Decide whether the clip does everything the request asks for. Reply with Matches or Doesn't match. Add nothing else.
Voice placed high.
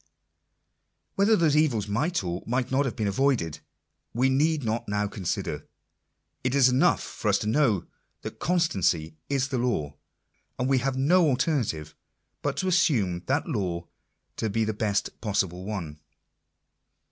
Doesn't match